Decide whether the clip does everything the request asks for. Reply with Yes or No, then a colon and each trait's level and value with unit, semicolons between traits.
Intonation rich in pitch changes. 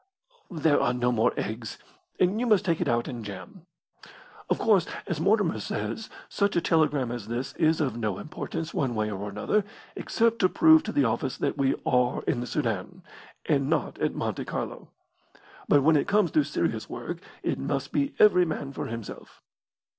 Yes: wide, 7.6 semitones